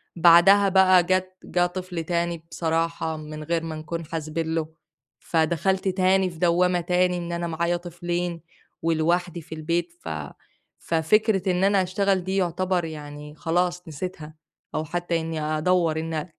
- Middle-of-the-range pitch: Yes, medium, 170 Hz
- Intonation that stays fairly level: Yes, narrow, 2.1 semitones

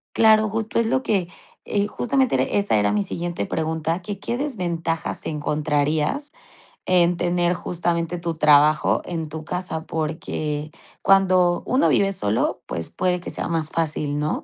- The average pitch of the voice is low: No, medium, 170 Hz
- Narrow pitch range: No, average, 4.0 semitones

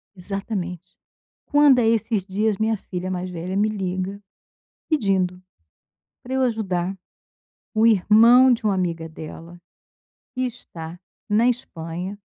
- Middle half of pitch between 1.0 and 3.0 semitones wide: No, average, 3.8 semitones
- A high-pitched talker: Yes, high, 195 Hz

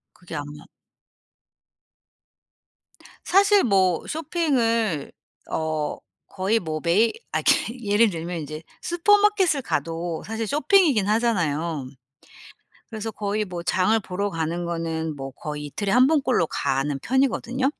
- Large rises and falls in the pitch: Yes, wide, 7.2 semitones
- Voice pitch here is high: Yes, high, 195 Hz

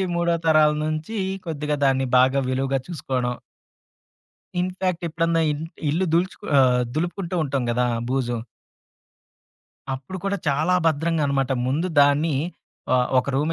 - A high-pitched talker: No, medium, 150 Hz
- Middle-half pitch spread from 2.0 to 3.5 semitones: No, average, 4.0 semitones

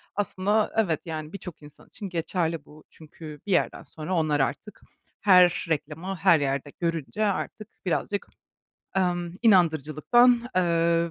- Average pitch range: Yes, average, 3.7 semitones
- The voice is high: No, medium, 170 Hz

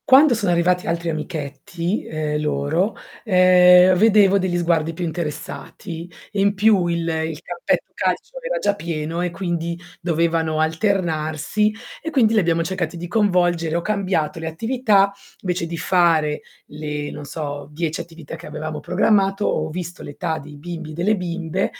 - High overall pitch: No, medium, 170 Hz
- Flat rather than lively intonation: No, average, 3.3 semitones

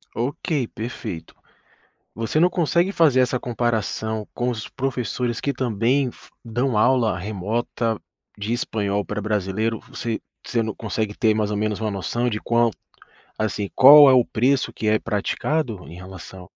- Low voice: Yes, low, 115 Hz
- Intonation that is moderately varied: Yes, average, 3.0 semitones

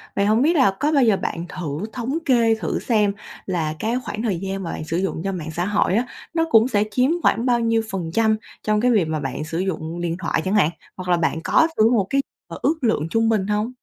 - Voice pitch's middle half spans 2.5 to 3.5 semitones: No, average, 4.9 semitones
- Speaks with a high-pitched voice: Yes, high, 205 Hz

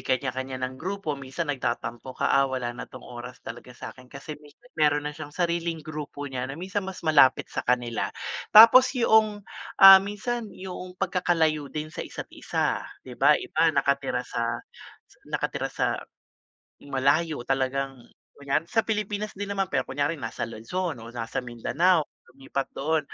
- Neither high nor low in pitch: Yes, medium, 150 Hz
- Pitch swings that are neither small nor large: No, wide, 5.9 semitones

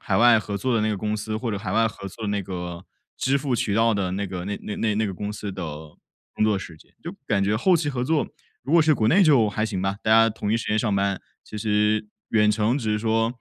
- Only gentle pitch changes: Yes, narrow, 2.1 semitones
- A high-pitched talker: No, low, 110 Hz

